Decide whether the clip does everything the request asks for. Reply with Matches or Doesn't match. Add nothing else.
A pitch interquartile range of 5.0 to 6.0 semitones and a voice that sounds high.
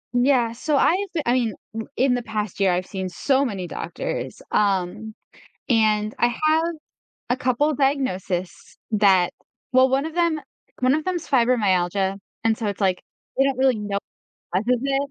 Matches